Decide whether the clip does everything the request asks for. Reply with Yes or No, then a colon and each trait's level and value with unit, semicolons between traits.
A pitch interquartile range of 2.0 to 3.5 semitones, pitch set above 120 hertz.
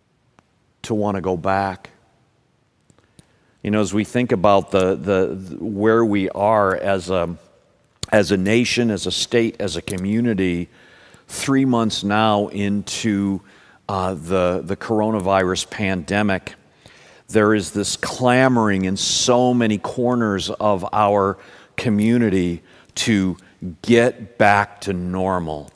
No: average, 3.0 semitones; low, 100 Hz